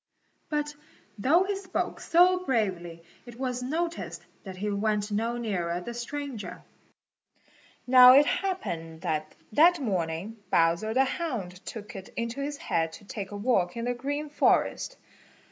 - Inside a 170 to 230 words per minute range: No, average, 145 wpm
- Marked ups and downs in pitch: Yes, wide, 7.2 semitones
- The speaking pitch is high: Yes, high, 235 Hz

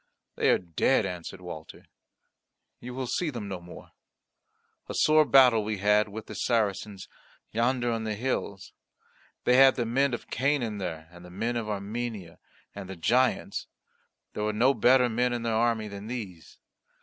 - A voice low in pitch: Yes, low, 110 Hz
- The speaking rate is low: No, average, 170 wpm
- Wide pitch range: No, average, 3.8 semitones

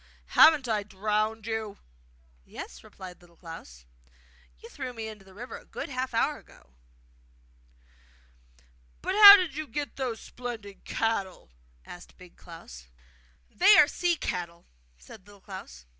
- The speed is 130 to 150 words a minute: Yes, average, 140 wpm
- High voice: Yes, high, 215 Hz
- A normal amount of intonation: No, wide, 6.2 semitones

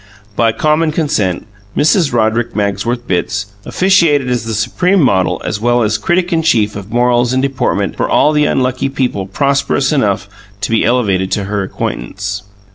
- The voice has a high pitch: No, low, 120 Hz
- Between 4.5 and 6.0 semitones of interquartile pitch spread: Yes, wide, 5.6 semitones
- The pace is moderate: Yes, average, 165 wpm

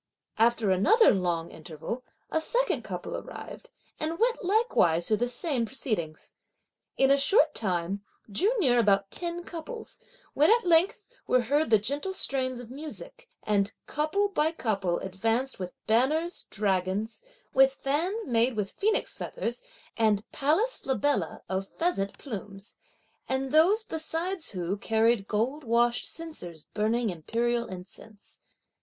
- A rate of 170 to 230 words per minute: No, slow, 135 wpm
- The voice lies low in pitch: No, high, 245 Hz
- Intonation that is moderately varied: No, wide, 8.0 semitones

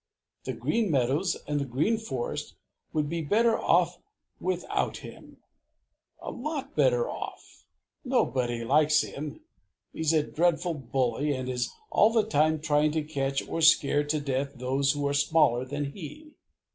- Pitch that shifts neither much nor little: Yes, average, 4.5 semitones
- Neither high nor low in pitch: Yes, medium, 150 Hz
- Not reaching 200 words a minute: Yes, average, 150 wpm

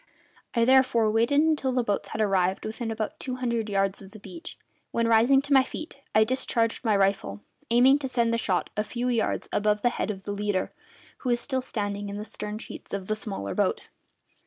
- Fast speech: Yes, fast, 210 wpm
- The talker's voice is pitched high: Yes, high, 225 Hz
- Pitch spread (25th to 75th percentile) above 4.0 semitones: No, average, 3.6 semitones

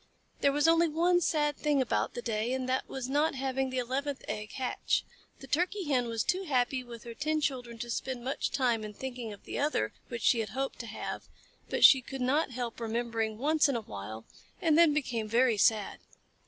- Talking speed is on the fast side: Yes, fast, 215 wpm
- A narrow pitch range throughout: No, average, 3.8 semitones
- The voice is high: Yes, very high, 255 Hz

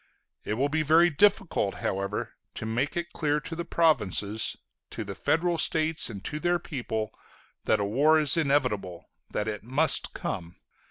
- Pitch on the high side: No, medium, 140 Hz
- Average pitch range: No, wide, 7.1 semitones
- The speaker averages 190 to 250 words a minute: No, average, 165 wpm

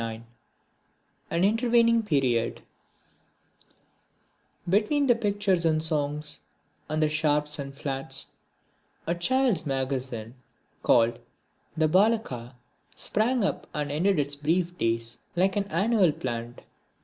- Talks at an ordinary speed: No, slow, 110 wpm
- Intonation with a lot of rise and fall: Yes, wide, 7.0 semitones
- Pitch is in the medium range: Yes, medium, 155 Hz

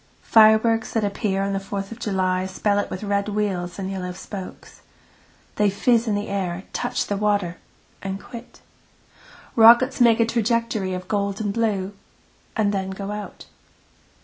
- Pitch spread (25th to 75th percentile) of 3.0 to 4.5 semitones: No, narrow, 2.5 semitones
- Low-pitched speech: No, high, 205 Hz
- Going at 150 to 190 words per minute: Yes, average, 165 wpm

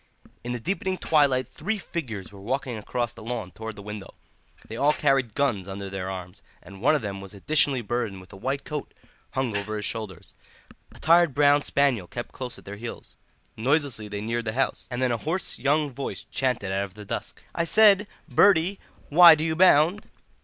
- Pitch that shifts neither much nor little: No, wide, 6.3 semitones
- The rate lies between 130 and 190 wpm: No, average, 200 wpm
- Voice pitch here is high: No, low, 125 Hz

